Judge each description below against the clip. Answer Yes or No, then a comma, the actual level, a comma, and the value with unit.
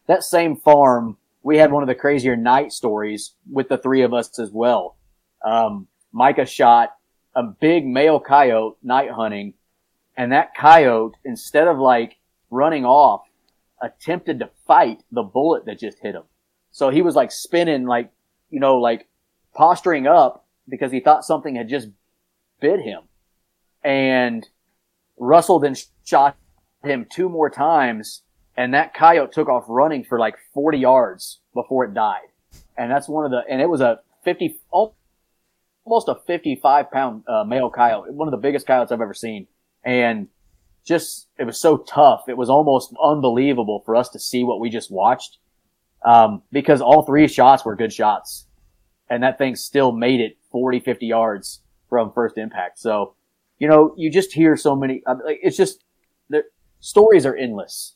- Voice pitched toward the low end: Yes, low, 130 Hz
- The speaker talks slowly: No, average, 170 wpm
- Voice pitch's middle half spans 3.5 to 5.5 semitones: Yes, average, 4.9 semitones